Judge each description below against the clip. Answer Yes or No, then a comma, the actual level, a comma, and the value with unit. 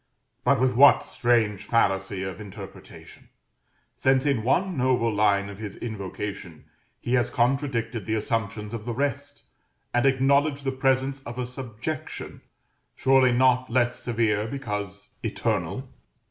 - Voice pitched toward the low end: Yes, low, 120 Hz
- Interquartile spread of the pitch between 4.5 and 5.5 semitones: No, average, 4.0 semitones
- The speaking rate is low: Yes, slow, 130 wpm